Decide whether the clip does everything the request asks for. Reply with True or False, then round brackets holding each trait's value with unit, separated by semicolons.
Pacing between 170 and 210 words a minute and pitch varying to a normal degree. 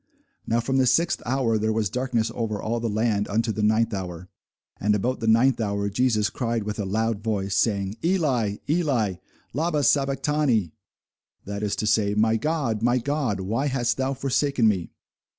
True (175 wpm; 4.0 semitones)